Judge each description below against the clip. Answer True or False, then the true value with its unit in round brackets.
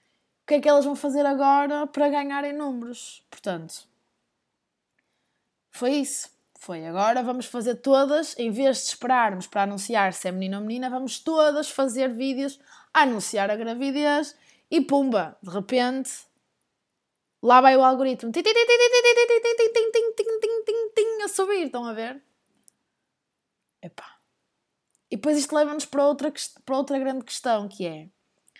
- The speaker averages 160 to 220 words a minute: False (150 wpm)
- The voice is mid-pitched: False (270 Hz)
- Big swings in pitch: False (4.0 semitones)